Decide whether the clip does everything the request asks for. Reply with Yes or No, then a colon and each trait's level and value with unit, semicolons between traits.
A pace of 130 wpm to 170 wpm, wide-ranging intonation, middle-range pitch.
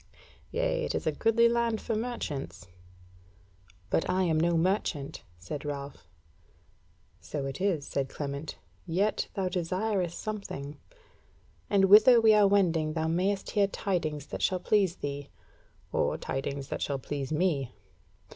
Yes: average, 140 wpm; wide, 6.0 semitones; medium, 175 Hz